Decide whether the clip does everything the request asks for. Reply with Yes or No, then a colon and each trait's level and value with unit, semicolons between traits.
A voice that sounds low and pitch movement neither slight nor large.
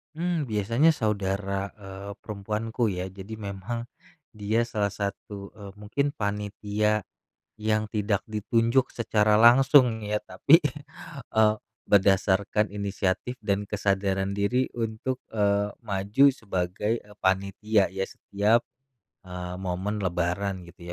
No: low, 105 Hz; narrow, 2.2 semitones